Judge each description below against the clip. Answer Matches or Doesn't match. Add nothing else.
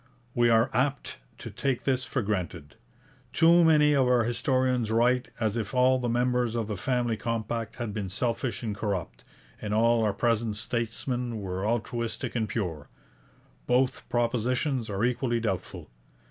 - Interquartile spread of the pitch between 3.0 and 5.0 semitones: Doesn't match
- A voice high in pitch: Doesn't match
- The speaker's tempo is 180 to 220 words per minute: Doesn't match